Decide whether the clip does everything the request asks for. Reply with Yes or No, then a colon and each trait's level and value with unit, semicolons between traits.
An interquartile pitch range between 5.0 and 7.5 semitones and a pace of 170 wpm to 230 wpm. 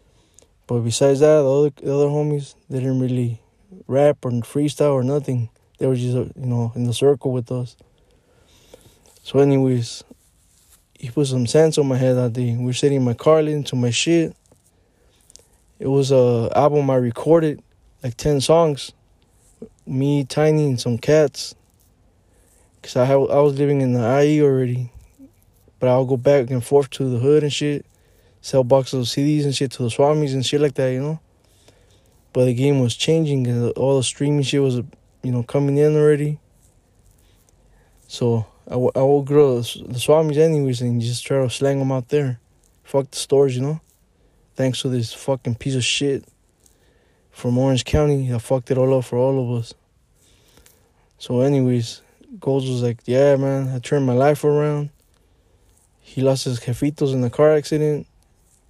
No: average, 3.0 semitones; average, 180 wpm